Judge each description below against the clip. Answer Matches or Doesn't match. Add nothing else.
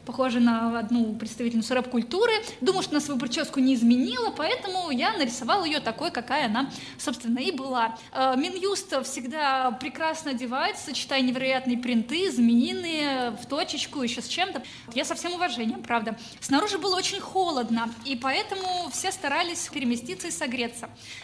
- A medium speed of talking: Matches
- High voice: Matches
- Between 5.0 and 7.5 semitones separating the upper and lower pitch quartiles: Matches